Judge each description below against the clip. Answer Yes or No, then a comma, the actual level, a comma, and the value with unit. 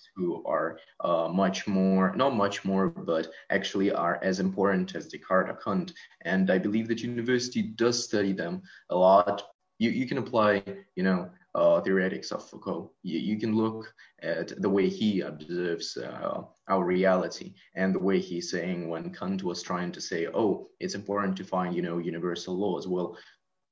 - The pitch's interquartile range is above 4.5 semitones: No, average, 2.7 semitones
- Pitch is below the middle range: Yes, very low, 95 Hz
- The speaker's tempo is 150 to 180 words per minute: Yes, average, 175 wpm